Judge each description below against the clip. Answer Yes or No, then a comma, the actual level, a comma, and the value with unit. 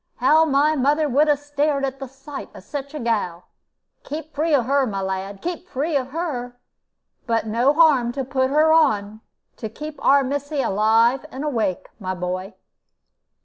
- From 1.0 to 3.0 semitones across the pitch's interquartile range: No, average, 4.7 semitones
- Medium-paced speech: Yes, average, 175 wpm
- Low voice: No, very high, 270 Hz